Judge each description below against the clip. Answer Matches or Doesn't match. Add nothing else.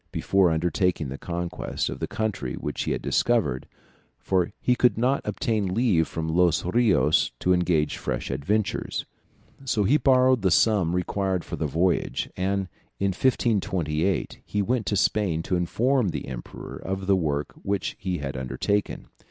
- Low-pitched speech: Matches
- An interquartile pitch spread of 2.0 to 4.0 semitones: Doesn't match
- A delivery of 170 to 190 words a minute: Doesn't match